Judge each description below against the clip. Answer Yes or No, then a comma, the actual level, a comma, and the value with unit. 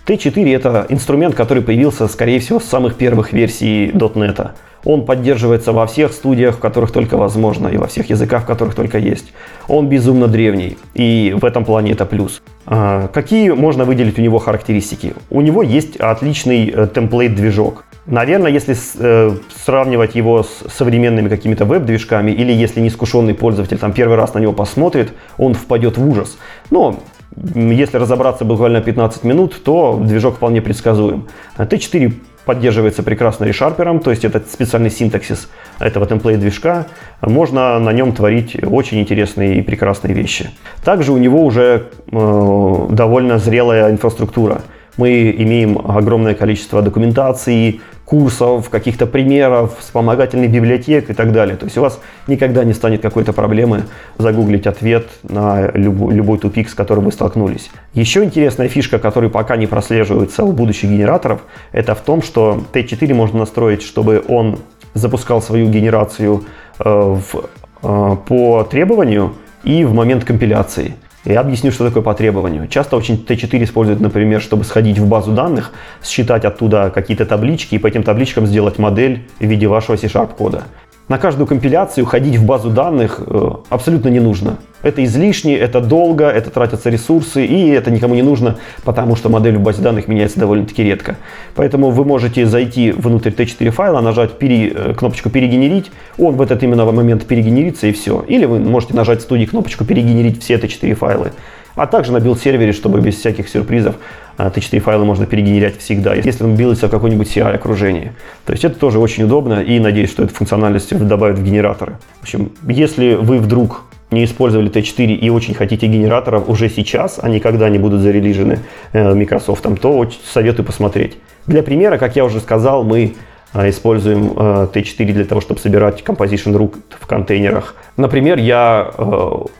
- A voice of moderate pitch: No, low, 115 Hz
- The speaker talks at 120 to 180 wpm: Yes, average, 155 wpm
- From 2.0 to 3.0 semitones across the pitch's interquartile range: Yes, average, 2.7 semitones